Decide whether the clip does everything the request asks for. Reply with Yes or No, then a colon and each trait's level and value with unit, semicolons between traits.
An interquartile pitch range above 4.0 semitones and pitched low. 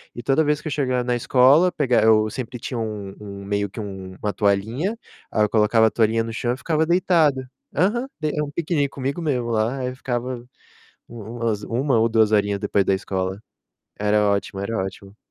Yes: average, 4.9 semitones; low, 115 Hz